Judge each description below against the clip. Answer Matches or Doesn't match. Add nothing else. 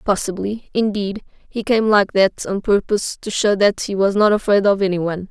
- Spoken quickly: Doesn't match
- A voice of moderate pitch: Doesn't match